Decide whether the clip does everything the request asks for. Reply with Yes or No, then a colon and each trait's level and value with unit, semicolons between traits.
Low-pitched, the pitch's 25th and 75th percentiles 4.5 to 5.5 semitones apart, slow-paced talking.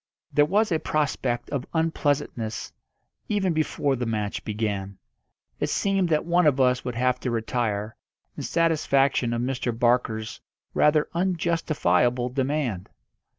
Yes: low, 130 Hz; average, 5.1 semitones; slow, 130 wpm